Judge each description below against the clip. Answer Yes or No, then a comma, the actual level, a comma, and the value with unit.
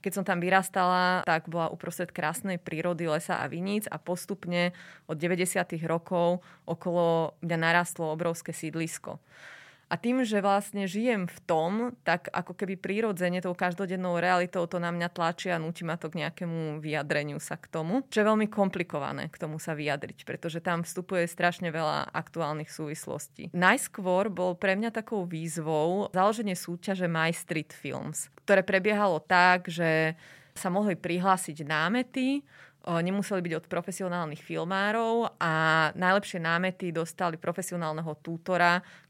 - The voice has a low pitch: No, medium, 175 Hz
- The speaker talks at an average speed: Yes, average, 145 wpm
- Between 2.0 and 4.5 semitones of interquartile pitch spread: Yes, narrow, 2.6 semitones